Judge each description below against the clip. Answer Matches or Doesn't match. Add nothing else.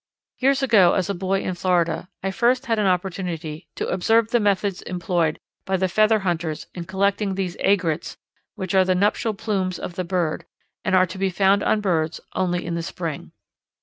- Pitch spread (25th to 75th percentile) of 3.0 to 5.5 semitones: Doesn't match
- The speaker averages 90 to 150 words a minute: Doesn't match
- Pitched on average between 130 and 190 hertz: Matches